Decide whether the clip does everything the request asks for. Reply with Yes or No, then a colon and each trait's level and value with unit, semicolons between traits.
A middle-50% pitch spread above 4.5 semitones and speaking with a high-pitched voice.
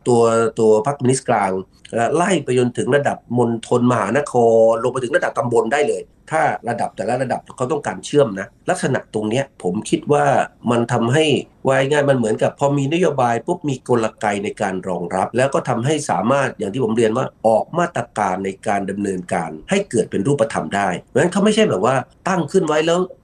No: average, 5.1 semitones; low, 125 Hz